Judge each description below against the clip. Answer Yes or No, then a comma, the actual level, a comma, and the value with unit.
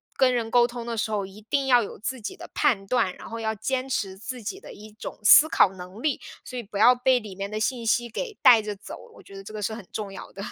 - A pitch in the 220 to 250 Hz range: Yes, high, 225 Hz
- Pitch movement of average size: Yes, average, 3.6 semitones